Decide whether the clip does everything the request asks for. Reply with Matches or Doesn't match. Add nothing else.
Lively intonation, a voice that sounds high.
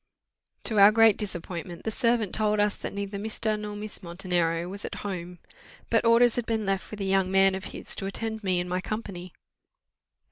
Doesn't match